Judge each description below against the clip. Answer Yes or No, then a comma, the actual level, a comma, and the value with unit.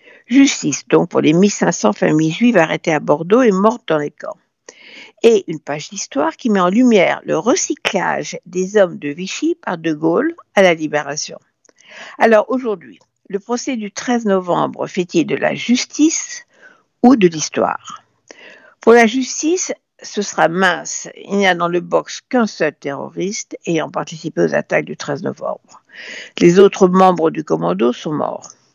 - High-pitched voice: Yes, high, 200 Hz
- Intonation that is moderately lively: No, wide, 7.2 semitones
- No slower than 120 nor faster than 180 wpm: Yes, average, 165 wpm